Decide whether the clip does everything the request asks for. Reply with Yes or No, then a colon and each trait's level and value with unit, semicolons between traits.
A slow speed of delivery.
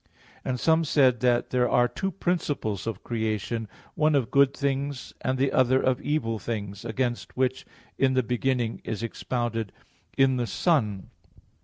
No: average, 155 wpm